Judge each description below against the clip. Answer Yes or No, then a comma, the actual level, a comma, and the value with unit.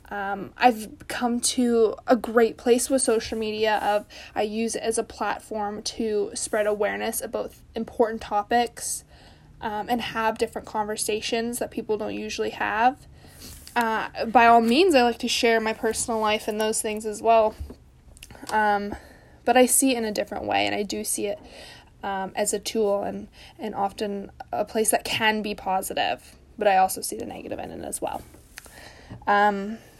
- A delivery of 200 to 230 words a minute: No, average, 175 wpm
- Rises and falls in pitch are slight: Yes, narrow, 2.0 semitones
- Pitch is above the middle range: Yes, high, 220 Hz